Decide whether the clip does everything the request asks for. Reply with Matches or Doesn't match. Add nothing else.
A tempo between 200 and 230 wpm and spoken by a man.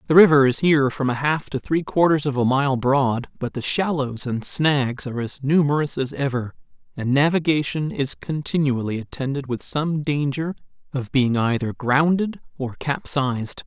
Doesn't match